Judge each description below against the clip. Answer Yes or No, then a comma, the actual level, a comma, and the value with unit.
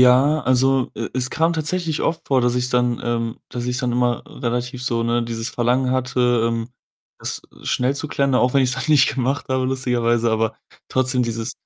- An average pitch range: No, narrow, 1.8 semitones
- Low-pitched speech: Yes, low, 125 Hz